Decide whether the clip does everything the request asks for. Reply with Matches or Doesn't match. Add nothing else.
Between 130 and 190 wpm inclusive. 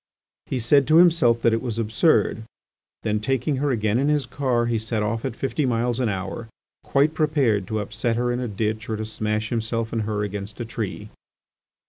Doesn't match